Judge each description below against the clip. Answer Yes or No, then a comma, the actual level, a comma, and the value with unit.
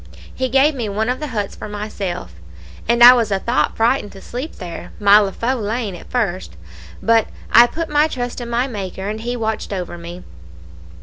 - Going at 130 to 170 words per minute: No, average, 195 wpm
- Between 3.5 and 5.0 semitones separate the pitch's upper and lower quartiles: Yes, average, 3.8 semitones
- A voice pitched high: Yes, high, 225 Hz